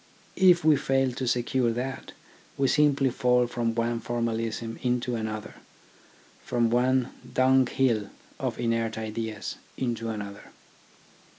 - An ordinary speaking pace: No, slow, 120 wpm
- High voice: No, low, 120 Hz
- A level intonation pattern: Yes, narrow, 2.3 semitones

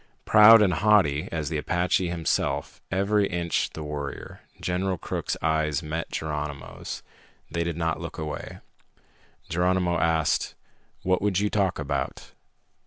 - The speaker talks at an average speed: No, slow, 130 wpm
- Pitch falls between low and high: No, very low, 85 Hz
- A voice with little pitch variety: No, average, 3.3 semitones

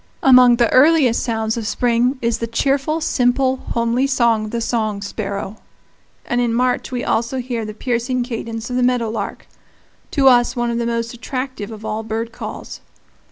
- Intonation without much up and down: Yes, narrow, 2.0 semitones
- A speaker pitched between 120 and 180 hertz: No, high, 235 Hz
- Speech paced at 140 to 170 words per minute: No, average, 180 wpm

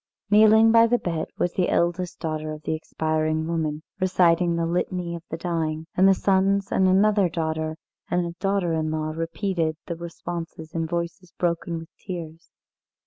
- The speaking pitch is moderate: Yes, medium, 170 Hz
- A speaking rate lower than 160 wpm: No, average, 170 wpm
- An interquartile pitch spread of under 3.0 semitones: Yes, narrow, 2.6 semitones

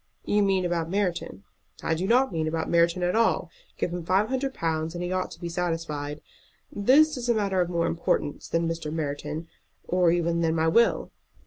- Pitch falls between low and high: Yes, medium, 170 Hz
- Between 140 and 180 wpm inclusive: No, average, 195 wpm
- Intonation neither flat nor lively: Yes, average, 3.0 semitones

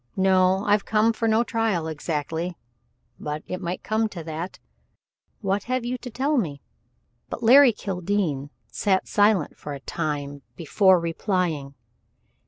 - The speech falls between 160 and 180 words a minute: No, average, 140 wpm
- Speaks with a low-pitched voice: No, medium, 185 Hz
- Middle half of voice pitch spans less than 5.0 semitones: No, average, 5.3 semitones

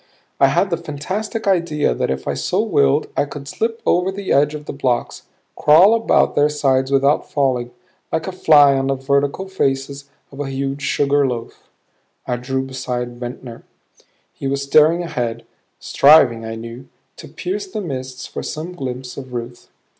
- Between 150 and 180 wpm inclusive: Yes, average, 170 wpm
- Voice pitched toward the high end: No, medium, 140 Hz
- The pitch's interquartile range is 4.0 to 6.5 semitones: No, average, 3.2 semitones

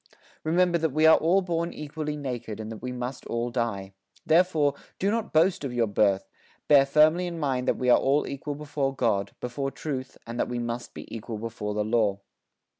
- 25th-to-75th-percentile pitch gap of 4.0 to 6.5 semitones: Yes, average, 5.0 semitones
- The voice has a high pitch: No, low, 135 Hz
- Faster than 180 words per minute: Yes, average, 200 wpm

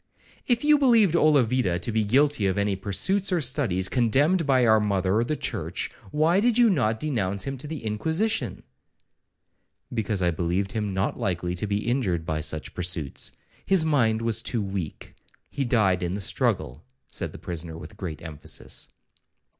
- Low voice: Yes, low, 110 Hz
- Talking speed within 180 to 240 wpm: No, average, 160 wpm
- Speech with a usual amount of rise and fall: No, wide, 7.9 semitones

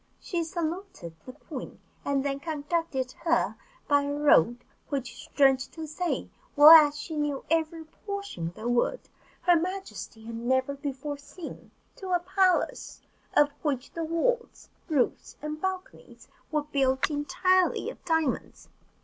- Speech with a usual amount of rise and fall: Yes, average, 3.7 semitones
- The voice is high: Yes, very high, 300 Hz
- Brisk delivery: No, average, 140 wpm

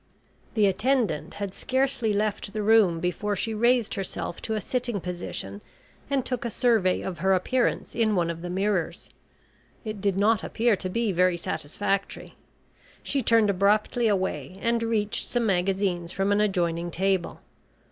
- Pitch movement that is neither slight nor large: Yes, average, 3.6 semitones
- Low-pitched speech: No, high, 200 Hz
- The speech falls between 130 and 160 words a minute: Yes, average, 155 wpm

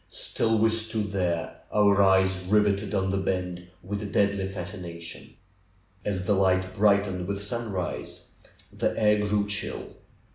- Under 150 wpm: Yes, average, 140 wpm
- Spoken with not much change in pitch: Yes, narrow, 1.9 semitones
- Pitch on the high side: No, low, 100 Hz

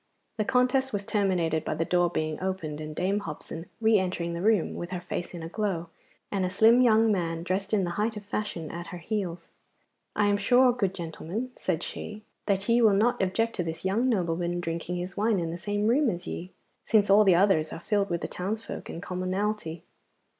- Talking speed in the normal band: No, fast, 210 wpm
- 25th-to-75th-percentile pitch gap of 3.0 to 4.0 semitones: Yes, average, 3.7 semitones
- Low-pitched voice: No, high, 190 Hz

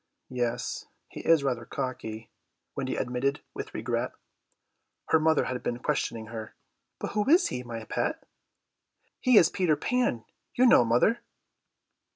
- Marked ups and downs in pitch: Yes, wide, 5.8 semitones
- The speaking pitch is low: Yes, low, 130 Hz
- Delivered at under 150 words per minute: Yes, average, 140 wpm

